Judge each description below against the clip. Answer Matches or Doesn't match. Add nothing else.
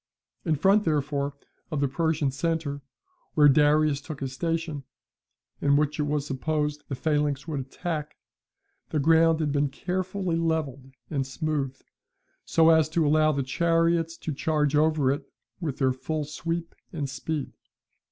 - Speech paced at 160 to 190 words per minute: Doesn't match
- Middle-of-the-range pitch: Matches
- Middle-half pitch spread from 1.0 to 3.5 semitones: Matches